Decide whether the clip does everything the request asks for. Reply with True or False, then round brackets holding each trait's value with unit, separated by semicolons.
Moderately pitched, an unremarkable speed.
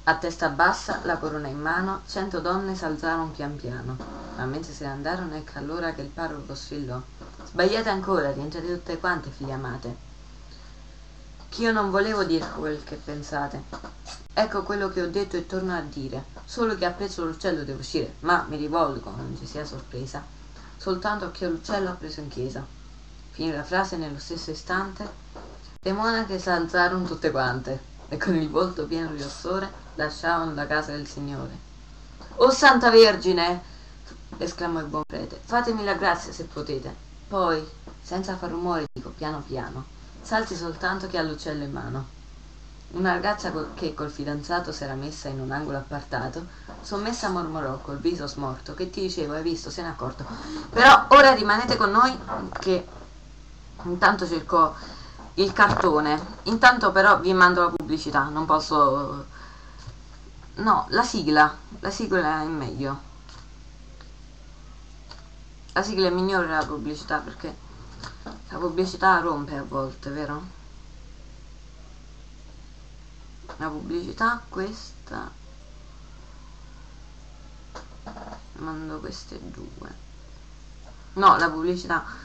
True (155 Hz; 140 wpm)